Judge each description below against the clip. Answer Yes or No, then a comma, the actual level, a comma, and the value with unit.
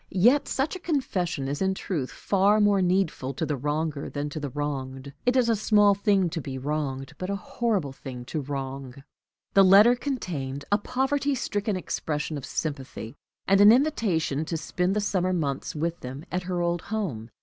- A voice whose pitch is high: No, medium, 175 Hz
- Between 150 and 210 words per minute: Yes, average, 180 wpm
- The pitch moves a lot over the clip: Yes, wide, 6.4 semitones